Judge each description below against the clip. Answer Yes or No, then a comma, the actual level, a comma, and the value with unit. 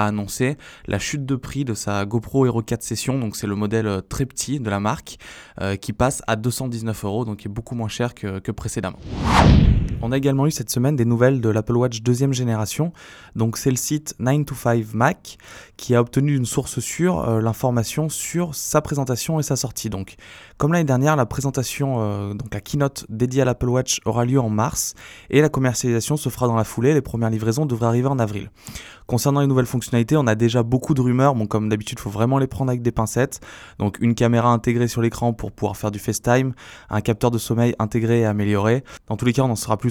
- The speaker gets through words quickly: Yes, fast, 225 wpm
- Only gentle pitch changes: No, average, 3.4 semitones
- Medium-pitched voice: No, low, 120 Hz